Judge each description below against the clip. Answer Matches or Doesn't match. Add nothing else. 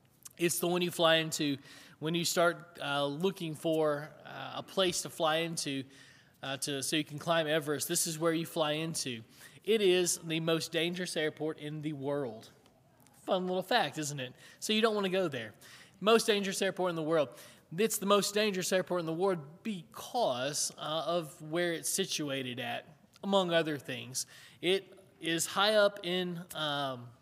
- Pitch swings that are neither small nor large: Matches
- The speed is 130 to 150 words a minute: Doesn't match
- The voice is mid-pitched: Matches